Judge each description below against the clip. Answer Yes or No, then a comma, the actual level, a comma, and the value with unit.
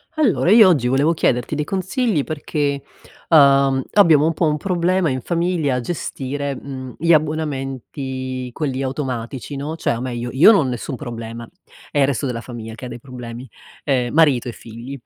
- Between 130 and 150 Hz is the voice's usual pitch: Yes, medium, 140 Hz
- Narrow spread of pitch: No, average, 3.8 semitones